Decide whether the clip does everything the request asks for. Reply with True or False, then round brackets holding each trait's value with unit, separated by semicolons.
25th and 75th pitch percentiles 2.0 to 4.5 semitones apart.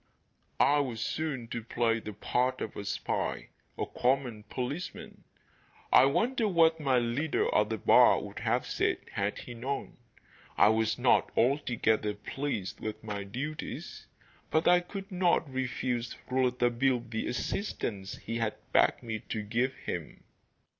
True (4.2 semitones)